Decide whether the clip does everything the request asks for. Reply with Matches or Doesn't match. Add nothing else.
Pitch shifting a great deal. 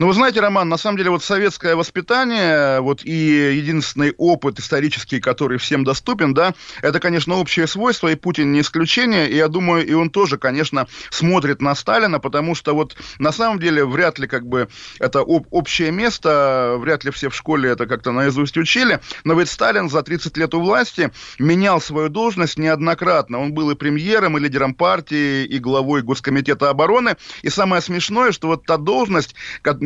Doesn't match